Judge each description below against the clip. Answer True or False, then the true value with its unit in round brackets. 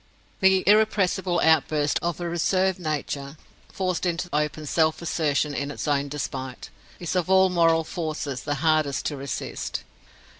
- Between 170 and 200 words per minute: False (145 wpm)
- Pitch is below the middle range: False (160 Hz)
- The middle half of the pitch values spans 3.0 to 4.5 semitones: True (3.6 semitones)